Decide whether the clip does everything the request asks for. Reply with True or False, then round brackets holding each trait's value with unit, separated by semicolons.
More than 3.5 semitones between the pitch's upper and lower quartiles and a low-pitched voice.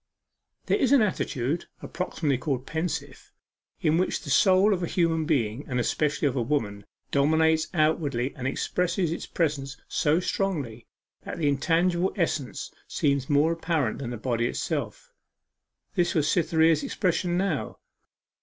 False (4.1 semitones; 155 Hz)